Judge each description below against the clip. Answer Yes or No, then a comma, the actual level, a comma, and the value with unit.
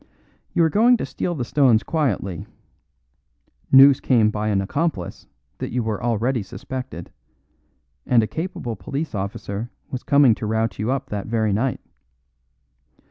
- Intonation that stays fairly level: No, average, 4.3 semitones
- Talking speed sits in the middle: Yes, average, 145 wpm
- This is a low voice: Yes, low, 120 Hz